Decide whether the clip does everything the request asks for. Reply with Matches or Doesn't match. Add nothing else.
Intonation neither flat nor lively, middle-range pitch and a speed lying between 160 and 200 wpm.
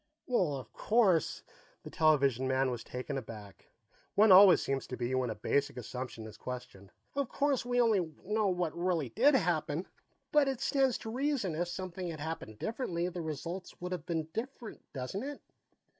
Doesn't match